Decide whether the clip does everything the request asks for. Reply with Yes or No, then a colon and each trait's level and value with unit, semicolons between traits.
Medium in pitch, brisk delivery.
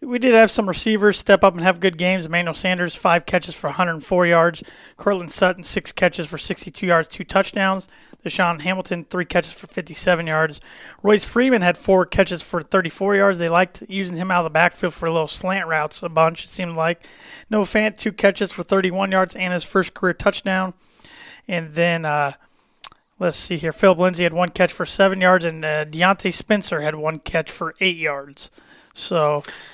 No: medium, 180 Hz; average, 195 wpm